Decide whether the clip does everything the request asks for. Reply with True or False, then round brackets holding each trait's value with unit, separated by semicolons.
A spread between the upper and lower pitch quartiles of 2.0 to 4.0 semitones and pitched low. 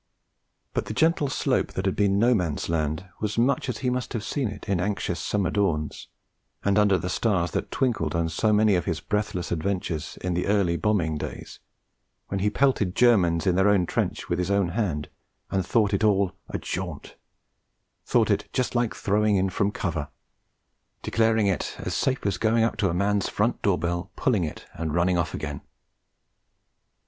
True (3.6 semitones; 100 Hz)